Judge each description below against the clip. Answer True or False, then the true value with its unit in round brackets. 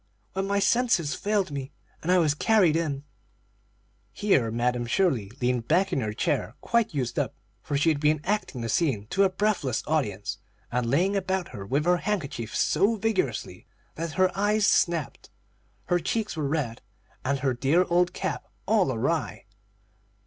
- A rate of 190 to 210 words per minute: False (165 wpm)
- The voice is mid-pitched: True (160 Hz)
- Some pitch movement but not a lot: False (6.7 semitones)